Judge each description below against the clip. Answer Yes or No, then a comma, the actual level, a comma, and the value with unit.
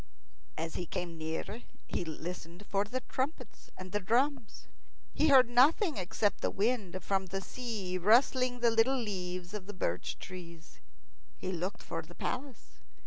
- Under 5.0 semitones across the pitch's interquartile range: No, wide, 5.5 semitones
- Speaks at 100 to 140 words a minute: No, average, 150 wpm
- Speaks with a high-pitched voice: Yes, high, 200 Hz